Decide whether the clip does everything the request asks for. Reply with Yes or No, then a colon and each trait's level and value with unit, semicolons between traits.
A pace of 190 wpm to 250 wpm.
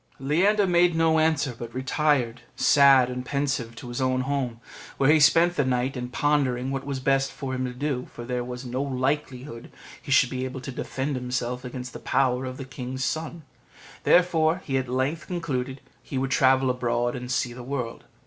Yes: average, 195 wpm